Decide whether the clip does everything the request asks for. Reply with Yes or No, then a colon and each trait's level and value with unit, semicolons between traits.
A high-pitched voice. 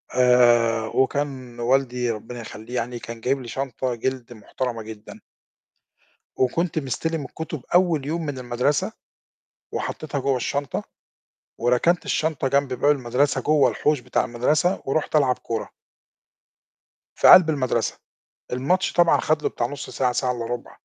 No: low, 130 Hz